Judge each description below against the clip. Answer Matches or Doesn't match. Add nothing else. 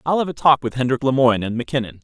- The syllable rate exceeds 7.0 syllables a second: Matches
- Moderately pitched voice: Doesn't match